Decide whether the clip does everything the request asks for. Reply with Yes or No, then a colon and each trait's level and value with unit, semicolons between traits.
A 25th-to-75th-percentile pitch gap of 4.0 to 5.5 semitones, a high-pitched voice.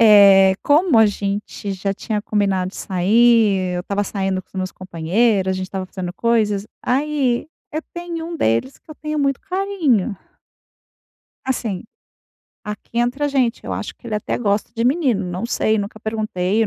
Yes: average, 4.6 semitones; high, 215 Hz